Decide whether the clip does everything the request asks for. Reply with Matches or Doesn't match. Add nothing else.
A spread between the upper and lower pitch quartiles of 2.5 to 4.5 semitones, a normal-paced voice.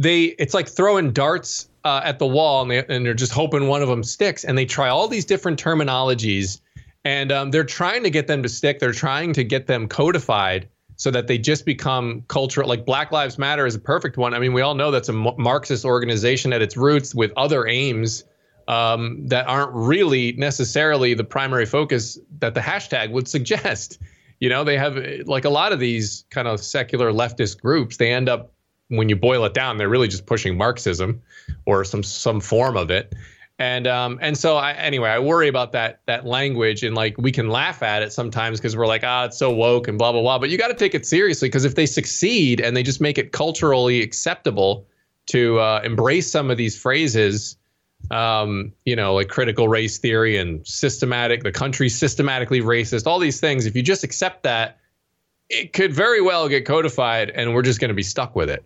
Doesn't match